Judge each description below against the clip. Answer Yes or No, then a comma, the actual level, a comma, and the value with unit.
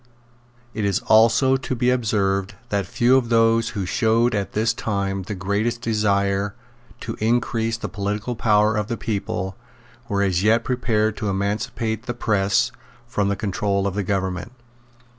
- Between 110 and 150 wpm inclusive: No, average, 160 wpm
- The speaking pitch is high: No, low, 105 Hz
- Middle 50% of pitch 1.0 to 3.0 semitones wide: Yes, narrow, 2.6 semitones